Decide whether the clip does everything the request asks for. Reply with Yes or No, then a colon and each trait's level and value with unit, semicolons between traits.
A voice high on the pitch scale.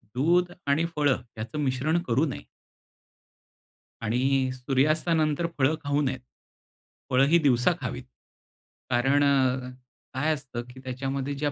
No: low, 135 Hz